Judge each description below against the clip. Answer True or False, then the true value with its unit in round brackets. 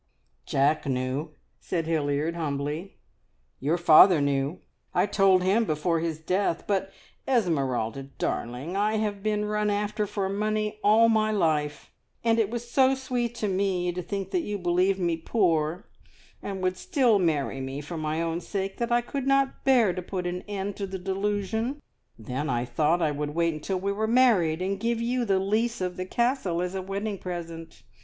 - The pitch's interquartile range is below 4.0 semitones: False (4.7 semitones)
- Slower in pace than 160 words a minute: False (180 wpm)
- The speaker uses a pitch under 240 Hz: True (190 Hz)